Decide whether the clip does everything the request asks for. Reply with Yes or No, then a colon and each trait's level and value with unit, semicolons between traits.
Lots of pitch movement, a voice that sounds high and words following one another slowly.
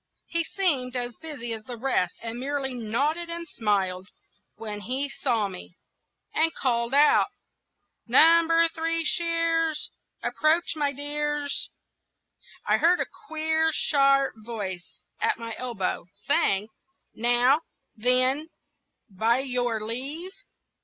Yes: wide, 5.7 semitones; very high, 270 Hz; slow, 115 wpm